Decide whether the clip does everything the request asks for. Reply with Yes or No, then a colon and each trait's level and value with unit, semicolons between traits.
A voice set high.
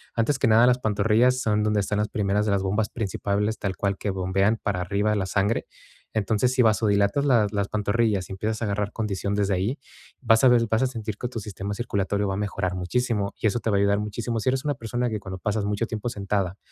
No: low, 105 Hz